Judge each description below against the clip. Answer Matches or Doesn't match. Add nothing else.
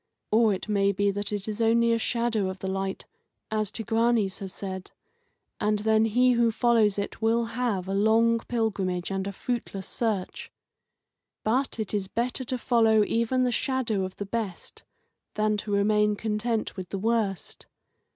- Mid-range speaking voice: Doesn't match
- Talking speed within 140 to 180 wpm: Matches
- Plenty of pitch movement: Doesn't match